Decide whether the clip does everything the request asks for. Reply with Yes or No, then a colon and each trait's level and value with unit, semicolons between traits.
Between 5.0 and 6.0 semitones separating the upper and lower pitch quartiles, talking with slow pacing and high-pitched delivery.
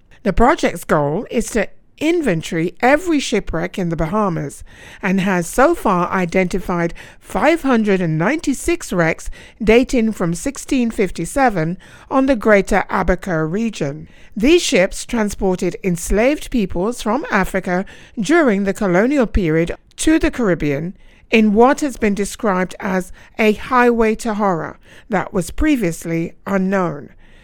Yes: average, 5.3 semitones; slow, 120 wpm; high, 200 Hz